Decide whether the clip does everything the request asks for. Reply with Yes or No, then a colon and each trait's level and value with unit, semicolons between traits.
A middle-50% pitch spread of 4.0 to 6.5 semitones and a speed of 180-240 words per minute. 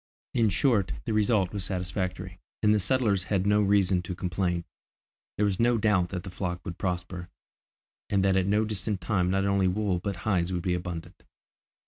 No: narrow, 2.4 semitones; average, 185 wpm